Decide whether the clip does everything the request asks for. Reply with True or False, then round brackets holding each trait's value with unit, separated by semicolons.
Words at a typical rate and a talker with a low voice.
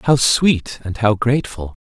True (165 wpm; 120 Hz)